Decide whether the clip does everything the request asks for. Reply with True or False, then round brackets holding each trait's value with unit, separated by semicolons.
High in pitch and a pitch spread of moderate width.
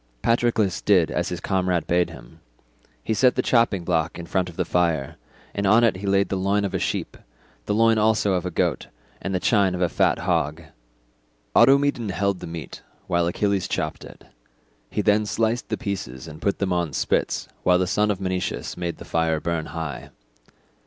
False (95 Hz; 3.4 semitones)